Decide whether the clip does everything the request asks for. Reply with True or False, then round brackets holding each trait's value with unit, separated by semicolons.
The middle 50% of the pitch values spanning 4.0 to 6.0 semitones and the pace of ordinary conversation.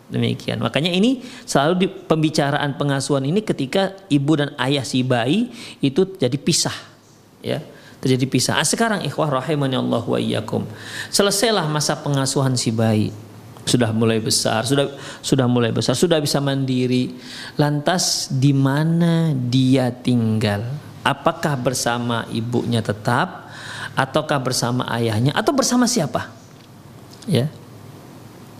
True (4.3 semitones; 120 wpm)